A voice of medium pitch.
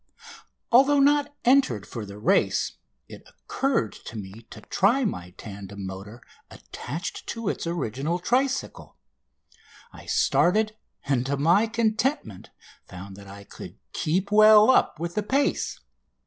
Yes: medium, 170 Hz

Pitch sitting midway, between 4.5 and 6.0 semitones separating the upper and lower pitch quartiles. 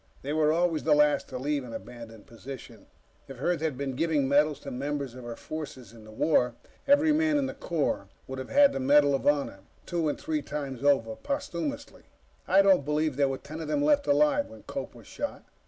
Yes: medium, 150 Hz; average, 4.9 semitones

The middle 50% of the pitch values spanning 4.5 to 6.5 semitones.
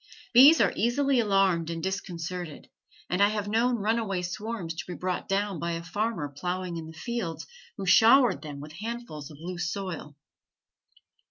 Yes: average, 4.8 semitones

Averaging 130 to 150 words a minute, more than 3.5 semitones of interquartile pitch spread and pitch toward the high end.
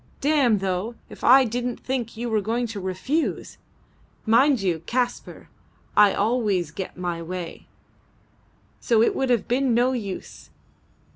Yes: average, 140 wpm; average, 4.4 semitones; high, 230 Hz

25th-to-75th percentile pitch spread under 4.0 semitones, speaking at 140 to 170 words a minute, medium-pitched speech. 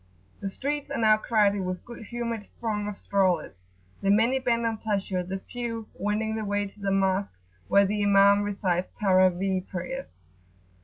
No: narrow, 2.5 semitones; average, 165 wpm; high, 205 Hz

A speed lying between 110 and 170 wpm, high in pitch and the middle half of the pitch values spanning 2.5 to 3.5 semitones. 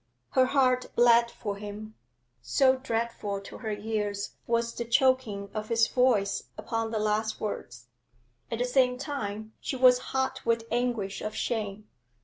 Yes: average, 150 wpm; high, 230 Hz; average, 3.0 semitones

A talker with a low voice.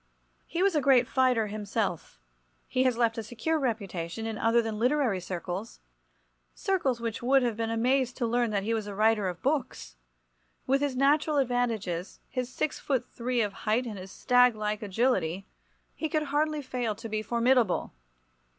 No: high, 235 Hz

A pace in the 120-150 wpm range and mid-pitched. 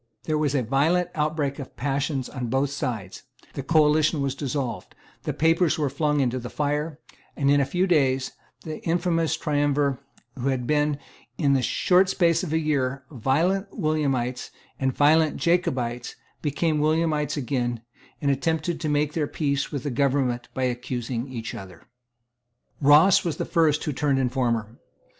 No: average, 160 wpm; medium, 145 Hz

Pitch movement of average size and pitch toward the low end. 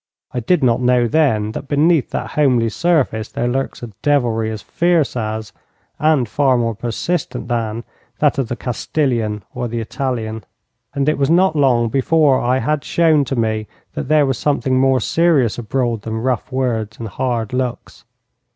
Yes: average, 4.0 semitones; low, 125 Hz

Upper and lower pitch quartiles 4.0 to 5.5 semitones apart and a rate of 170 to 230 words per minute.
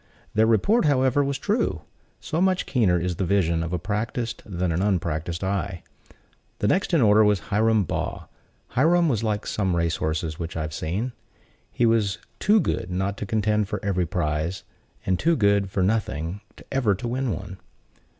Yes: average, 4.8 semitones; average, 180 wpm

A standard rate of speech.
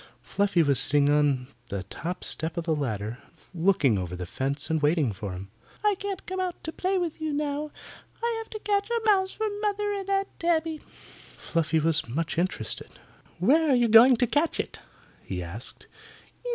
Yes: average, 185 wpm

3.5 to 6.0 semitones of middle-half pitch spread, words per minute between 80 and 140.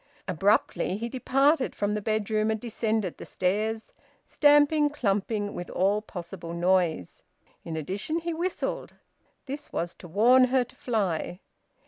Yes: wide, 5.5 semitones; slow, 135 wpm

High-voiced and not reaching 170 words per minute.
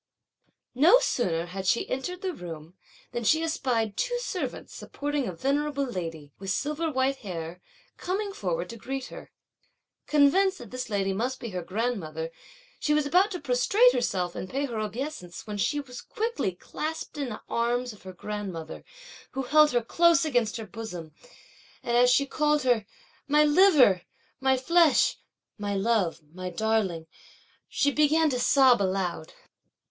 Yes: high, 245 Hz; average, 160 wpm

